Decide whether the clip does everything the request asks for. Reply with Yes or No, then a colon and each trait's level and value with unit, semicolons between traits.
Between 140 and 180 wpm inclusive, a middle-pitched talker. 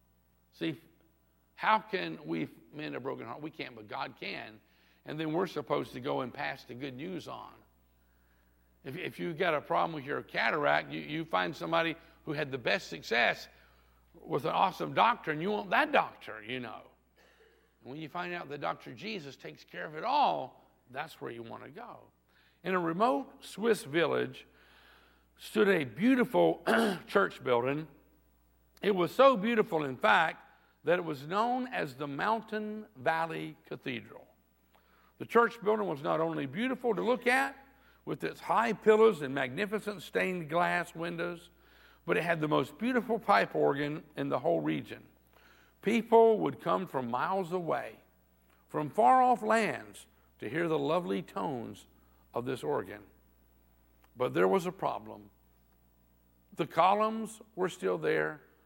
Yes: average, 160 wpm; medium, 155 Hz